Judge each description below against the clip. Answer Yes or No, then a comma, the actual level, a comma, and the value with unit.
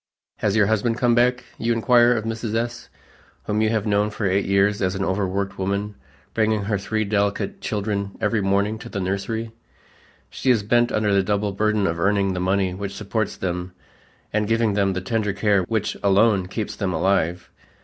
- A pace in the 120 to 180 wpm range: No, average, 190 wpm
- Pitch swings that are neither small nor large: No, narrow, 2.1 semitones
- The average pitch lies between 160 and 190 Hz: No, low, 105 Hz